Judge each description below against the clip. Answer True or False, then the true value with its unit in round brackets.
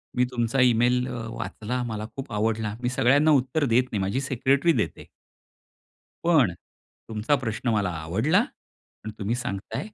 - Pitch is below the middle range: True (120 Hz)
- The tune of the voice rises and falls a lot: False (3.4 semitones)